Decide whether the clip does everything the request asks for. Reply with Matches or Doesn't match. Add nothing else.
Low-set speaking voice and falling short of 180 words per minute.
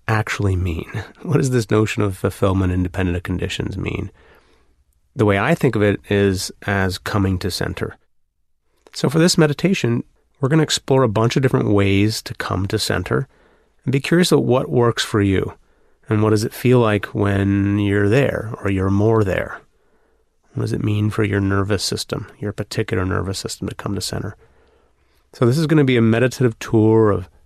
Doesn't match